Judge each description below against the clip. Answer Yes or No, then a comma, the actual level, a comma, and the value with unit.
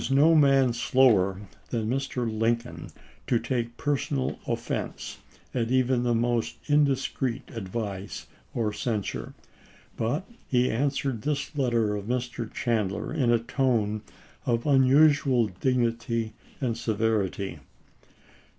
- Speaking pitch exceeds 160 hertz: No, low, 120 Hz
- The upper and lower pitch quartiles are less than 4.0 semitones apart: Yes, average, 2.9 semitones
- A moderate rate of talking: No, slow, 115 wpm